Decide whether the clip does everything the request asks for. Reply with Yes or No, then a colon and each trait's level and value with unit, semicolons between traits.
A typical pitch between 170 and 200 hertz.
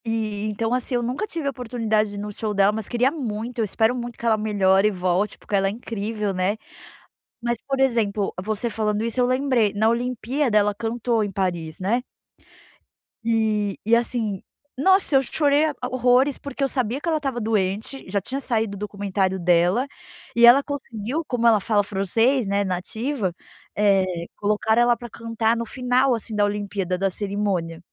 No: high, 220 Hz